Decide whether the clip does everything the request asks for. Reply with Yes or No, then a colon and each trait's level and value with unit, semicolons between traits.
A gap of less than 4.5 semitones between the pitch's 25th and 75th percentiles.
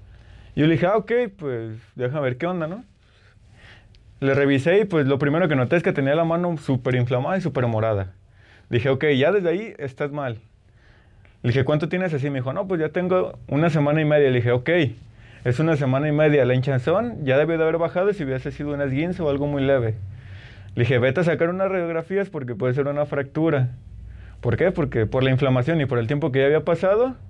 No: average, 5.2 semitones